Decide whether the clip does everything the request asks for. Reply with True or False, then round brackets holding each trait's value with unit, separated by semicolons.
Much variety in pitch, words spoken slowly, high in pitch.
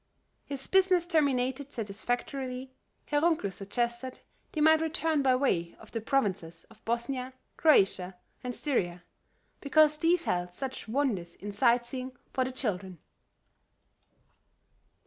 True (5.7 semitones; 120 wpm; 255 Hz)